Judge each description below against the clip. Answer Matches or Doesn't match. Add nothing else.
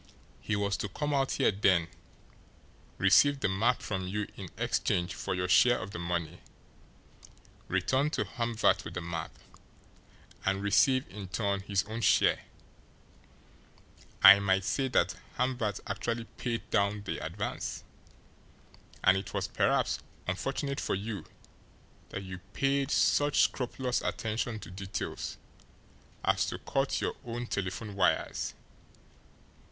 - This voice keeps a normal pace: Doesn't match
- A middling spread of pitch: Matches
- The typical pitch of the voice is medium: Doesn't match